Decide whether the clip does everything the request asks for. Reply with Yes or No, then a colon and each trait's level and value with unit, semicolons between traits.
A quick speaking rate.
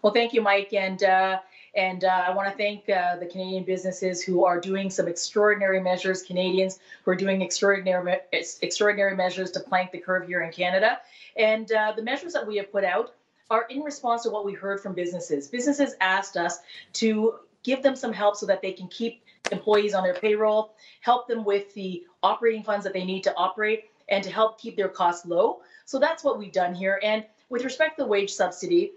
Yes: fast, 215 wpm